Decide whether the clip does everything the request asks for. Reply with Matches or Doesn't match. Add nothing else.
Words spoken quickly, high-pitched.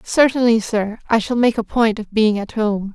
Matches